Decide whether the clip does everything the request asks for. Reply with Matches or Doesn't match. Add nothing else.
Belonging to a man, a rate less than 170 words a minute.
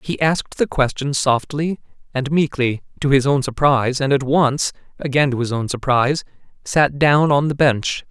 Doesn't match